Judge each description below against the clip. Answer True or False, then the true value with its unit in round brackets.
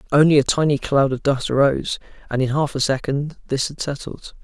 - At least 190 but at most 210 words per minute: True (205 wpm)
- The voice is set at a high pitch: False (140 Hz)